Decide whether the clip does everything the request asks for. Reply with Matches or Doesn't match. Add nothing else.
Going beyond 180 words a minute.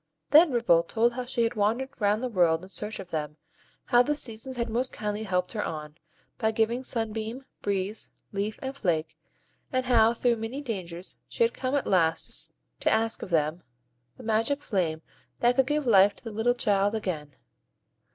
Matches